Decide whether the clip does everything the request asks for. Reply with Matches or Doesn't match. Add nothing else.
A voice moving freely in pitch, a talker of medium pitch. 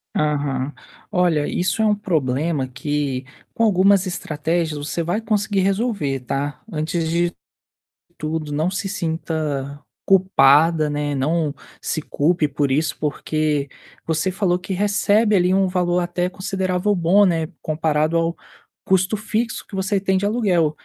Doesn't match